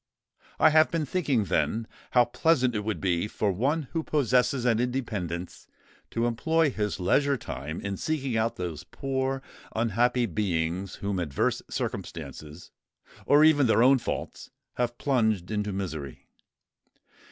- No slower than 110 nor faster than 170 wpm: Yes, average, 140 wpm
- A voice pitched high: No, low, 115 Hz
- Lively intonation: Yes, wide, 5.7 semitones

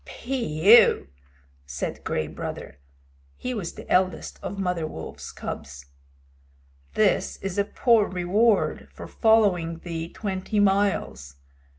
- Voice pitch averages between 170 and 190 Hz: Yes, medium, 185 Hz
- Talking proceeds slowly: Yes, slow, 110 wpm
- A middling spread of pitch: Yes, average, 4.2 semitones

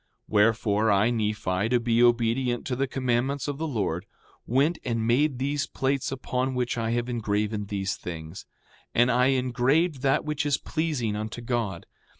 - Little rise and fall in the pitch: No, average, 3.7 semitones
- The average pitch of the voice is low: Yes, low, 120 Hz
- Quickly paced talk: No, average, 170 wpm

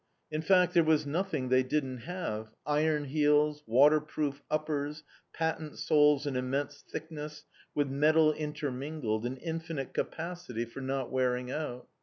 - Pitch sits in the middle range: Yes, medium, 150 Hz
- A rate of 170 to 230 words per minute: No, slow, 135 wpm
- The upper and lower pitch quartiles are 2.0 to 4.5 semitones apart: Yes, average, 2.8 semitones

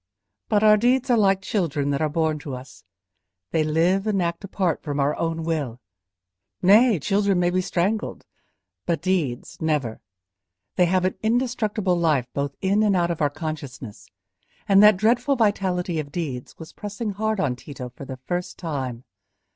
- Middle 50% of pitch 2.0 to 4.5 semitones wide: No, wide, 5.5 semitones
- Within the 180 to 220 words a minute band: No, average, 170 wpm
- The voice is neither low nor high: Yes, medium, 175 Hz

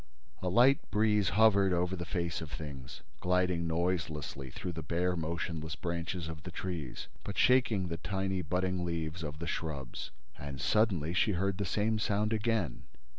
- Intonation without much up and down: No, average, 3.3 semitones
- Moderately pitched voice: No, very low, 90 Hz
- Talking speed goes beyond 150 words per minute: Yes, average, 165 wpm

